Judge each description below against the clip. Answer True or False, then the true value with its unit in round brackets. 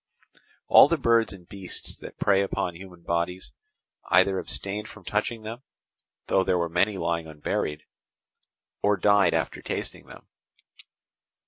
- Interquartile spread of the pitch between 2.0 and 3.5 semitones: True (3.2 semitones)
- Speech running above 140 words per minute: False (135 wpm)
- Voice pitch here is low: True (95 Hz)